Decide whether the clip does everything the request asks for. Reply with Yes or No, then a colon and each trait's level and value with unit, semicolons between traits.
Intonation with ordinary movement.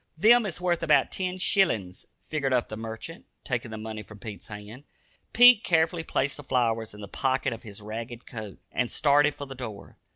No: wide, 6.6 semitones